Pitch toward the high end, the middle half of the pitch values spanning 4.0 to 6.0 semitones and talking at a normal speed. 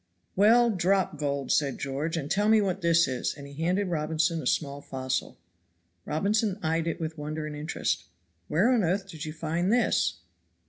No: medium, 165 Hz; average, 4.4 semitones; average, 180 wpm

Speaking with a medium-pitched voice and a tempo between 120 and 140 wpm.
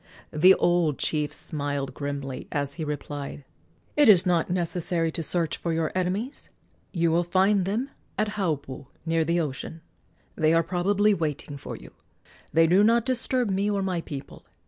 No: medium, 170 Hz; average, 165 wpm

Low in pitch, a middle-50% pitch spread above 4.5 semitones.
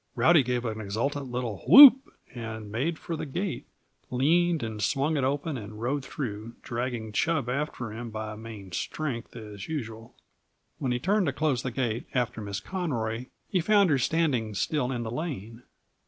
Yes: low, 125 Hz; average, 5.3 semitones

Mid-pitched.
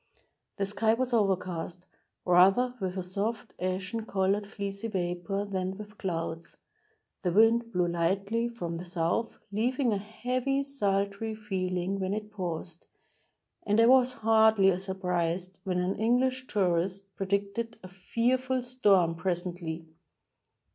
No: high, 195 Hz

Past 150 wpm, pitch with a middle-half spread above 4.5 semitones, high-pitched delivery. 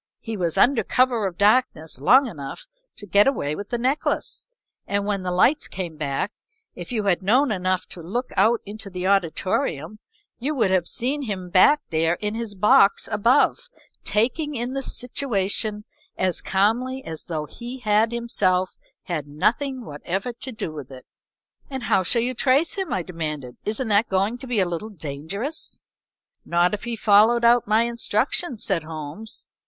Yes: average, 170 wpm; average, 5.1 semitones; high, 210 Hz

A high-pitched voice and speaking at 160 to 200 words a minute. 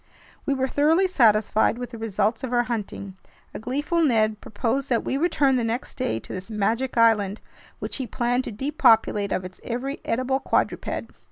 Yes: high, 240 Hz; average, 180 wpm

